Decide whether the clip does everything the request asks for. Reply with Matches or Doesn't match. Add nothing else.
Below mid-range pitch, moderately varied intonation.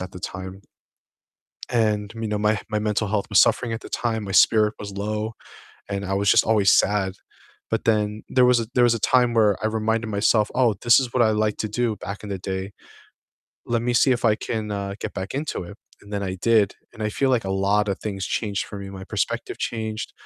Doesn't match